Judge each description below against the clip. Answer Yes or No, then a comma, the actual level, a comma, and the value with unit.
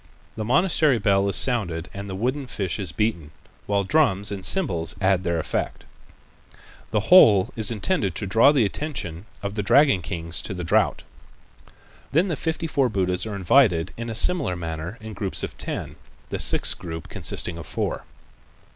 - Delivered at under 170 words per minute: No, average, 175 wpm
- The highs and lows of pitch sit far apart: Yes, wide, 5.7 semitones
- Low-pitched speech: Yes, low, 100 Hz